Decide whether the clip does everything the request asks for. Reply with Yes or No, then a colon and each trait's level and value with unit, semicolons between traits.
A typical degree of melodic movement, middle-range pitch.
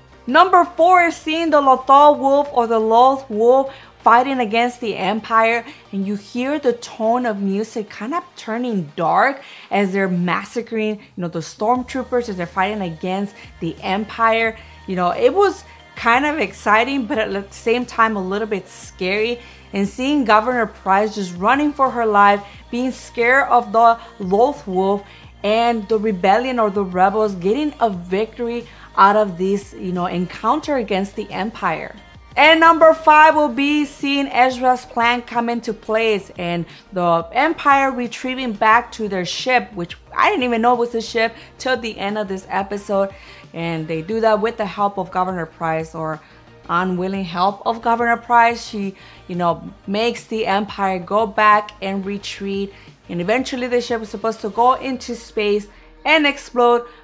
No: average, 3.8 semitones; high, 225 Hz